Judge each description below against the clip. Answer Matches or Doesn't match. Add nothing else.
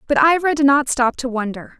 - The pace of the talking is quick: Matches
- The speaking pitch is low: Doesn't match